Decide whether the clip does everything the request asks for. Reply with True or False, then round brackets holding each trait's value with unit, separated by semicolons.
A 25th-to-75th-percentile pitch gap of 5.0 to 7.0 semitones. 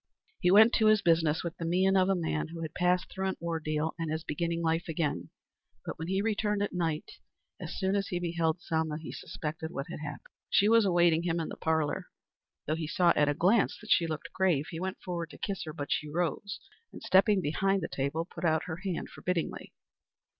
False (3.0 semitones)